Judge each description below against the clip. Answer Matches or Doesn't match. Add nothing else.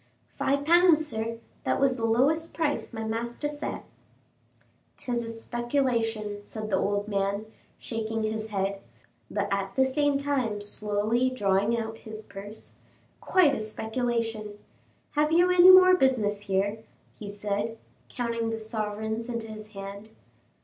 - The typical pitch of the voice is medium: Doesn't match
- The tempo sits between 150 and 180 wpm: Doesn't match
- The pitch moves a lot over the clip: Doesn't match